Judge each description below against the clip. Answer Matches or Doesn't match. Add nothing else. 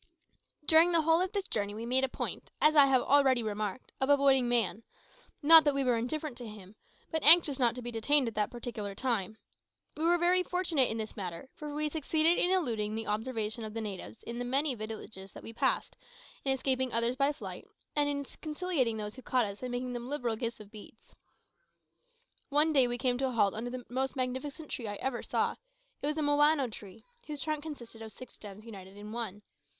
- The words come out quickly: Matches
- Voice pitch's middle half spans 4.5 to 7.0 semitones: Matches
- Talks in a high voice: Matches